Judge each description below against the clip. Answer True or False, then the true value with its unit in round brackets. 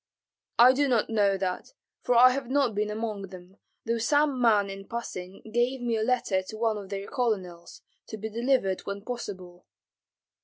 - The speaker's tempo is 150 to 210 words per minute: True (180 wpm)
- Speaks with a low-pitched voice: False (220 Hz)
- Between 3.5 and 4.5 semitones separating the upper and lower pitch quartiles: True (3.8 semitones)